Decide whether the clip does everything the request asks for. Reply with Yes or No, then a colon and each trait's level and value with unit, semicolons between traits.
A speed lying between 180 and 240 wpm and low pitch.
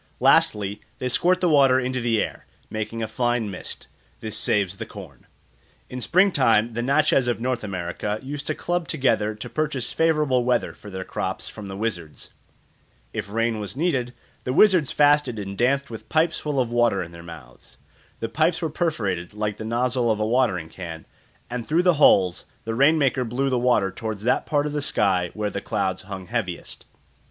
Yes: average, 190 wpm; low, 120 Hz